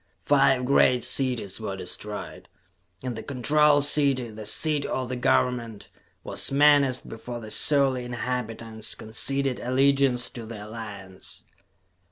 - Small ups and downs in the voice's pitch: No, average, 3.6 semitones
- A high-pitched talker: No, low, 125 Hz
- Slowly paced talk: Yes, slow, 125 wpm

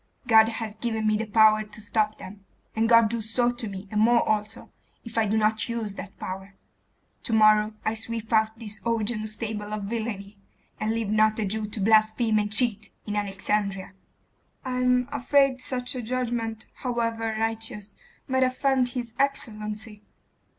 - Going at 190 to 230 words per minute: No, average, 170 wpm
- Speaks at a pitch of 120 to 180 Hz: No, high, 220 Hz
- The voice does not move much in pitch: Yes, narrow, 1.7 semitones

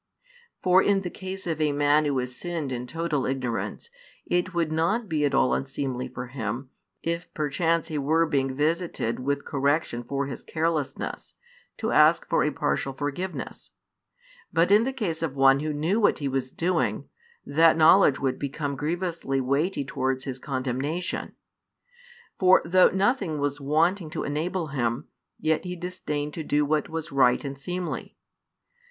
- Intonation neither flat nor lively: Yes, average, 3.9 semitones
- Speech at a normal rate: Yes, average, 160 wpm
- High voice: No, medium, 150 Hz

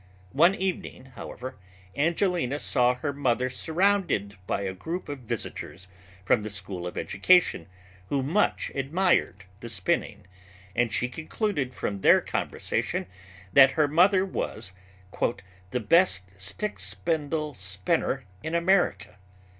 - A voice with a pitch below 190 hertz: Yes, medium, 140 Hz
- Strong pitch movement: Yes, wide, 8.1 semitones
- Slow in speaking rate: Yes, slow, 120 wpm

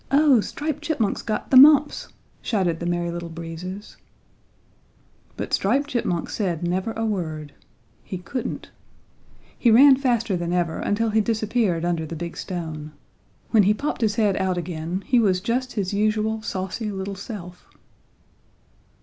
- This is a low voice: No, high, 200 Hz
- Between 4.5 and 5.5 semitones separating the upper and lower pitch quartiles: Yes, average, 4.8 semitones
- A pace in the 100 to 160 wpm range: Yes, average, 150 wpm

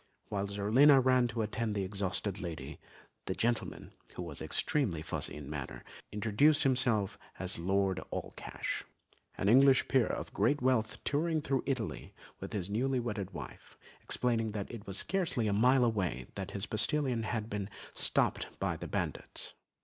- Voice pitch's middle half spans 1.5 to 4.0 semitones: No, average, 4.6 semitones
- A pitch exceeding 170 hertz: No, low, 110 Hz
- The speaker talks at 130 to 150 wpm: No, average, 160 wpm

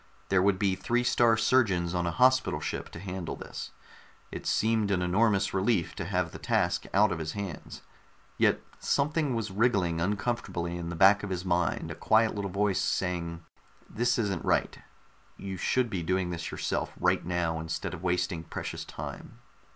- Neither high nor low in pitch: No, very low, 95 Hz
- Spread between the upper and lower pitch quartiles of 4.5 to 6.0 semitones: No, average, 3.6 semitones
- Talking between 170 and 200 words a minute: Yes, average, 175 wpm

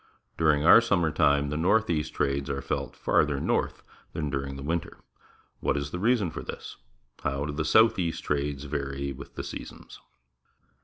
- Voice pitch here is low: Yes, very low, 75 Hz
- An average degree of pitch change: Yes, average, 3.1 semitones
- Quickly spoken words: No, average, 175 wpm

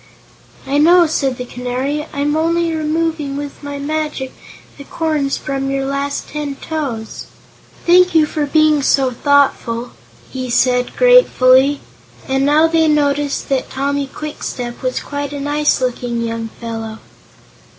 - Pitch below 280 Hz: No, very high, 285 Hz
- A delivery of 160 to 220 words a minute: No, average, 140 wpm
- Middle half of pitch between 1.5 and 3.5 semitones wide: Yes, average, 2.8 semitones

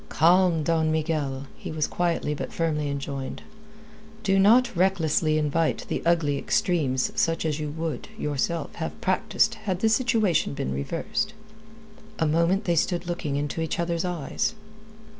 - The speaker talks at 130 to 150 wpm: Yes, average, 145 wpm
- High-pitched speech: No, medium, 165 Hz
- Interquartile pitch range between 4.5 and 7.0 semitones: No, average, 3.0 semitones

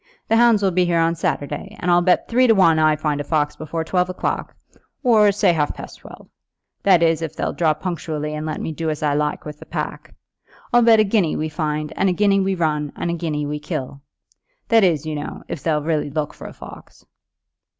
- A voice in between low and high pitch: Yes, medium, 165 Hz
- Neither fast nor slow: No, fast, 230 wpm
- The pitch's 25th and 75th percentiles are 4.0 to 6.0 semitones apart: No, average, 3.6 semitones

